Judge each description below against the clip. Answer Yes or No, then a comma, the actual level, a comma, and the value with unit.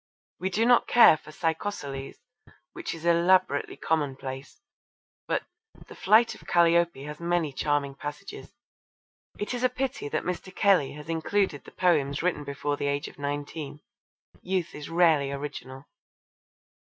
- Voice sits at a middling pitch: Yes, medium, 160 Hz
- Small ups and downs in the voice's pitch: No, average, 4.1 semitones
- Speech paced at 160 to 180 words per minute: No, average, 140 wpm